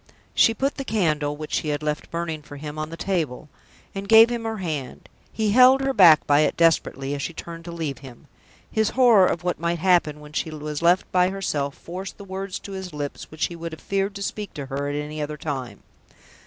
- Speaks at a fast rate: Yes, fast, 230 wpm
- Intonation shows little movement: No, average, 4.6 semitones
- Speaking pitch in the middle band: Yes, medium, 165 Hz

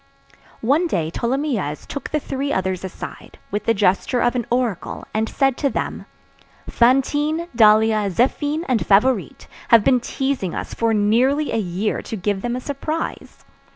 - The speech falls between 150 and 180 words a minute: Yes, average, 155 wpm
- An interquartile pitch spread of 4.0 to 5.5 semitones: Yes, average, 4.8 semitones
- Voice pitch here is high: Yes, high, 235 Hz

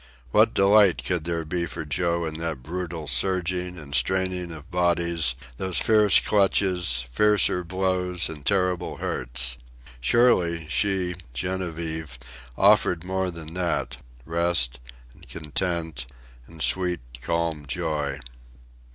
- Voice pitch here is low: Yes, very low, 85 Hz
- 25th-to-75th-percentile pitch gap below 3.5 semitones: Yes, average, 2.9 semitones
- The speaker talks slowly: Yes, slow, 115 wpm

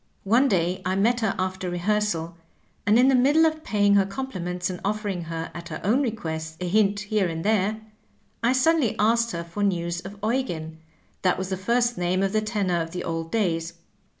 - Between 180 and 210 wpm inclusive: Yes, fast, 205 wpm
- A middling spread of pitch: Yes, average, 4.2 semitones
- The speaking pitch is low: No, high, 195 Hz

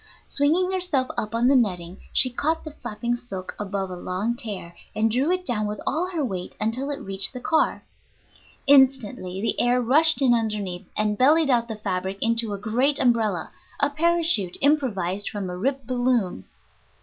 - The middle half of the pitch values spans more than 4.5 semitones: Yes, wide, 5.6 semitones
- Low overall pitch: No, high, 235 Hz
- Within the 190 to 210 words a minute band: No, average, 175 wpm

